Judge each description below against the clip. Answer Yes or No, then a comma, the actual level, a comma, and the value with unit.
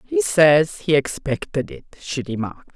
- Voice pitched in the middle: Yes, medium, 160 Hz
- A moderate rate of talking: Yes, average, 150 wpm